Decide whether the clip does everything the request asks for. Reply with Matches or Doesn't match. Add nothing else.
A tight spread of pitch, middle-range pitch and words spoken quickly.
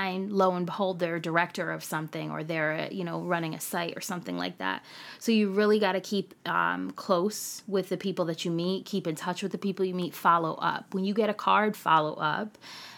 Doesn't match